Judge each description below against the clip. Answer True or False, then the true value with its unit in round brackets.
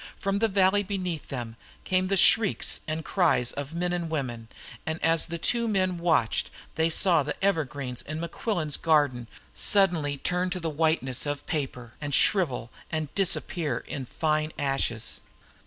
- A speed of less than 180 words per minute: True (155 wpm)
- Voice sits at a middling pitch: True (160 Hz)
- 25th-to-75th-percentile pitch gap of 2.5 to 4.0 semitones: False (4.4 semitones)